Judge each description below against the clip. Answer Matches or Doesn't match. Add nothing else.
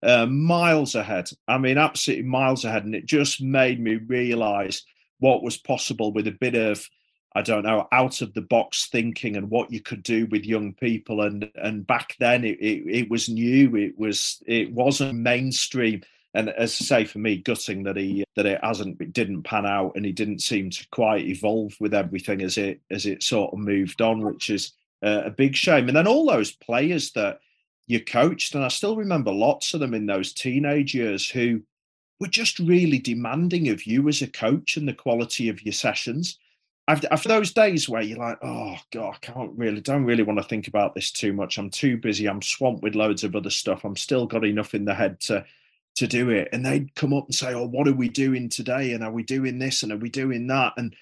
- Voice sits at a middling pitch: Doesn't match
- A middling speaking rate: Doesn't match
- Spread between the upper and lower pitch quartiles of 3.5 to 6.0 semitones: Matches